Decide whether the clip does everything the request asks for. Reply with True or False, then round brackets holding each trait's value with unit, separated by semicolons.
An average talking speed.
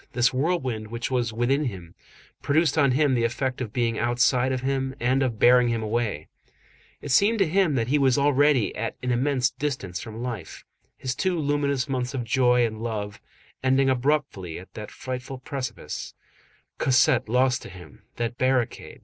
True (175 wpm)